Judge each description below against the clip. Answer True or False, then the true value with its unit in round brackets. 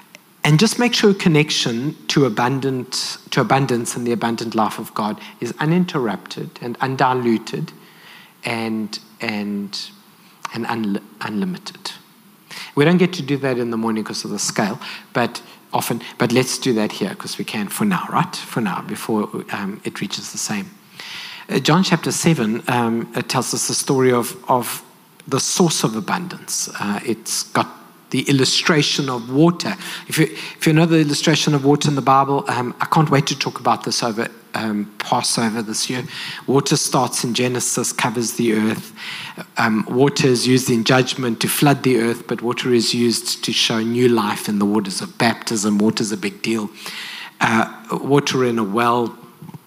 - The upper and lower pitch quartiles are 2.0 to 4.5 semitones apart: False (5.6 semitones)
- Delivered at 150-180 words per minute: True (175 wpm)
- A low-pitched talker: True (130 Hz)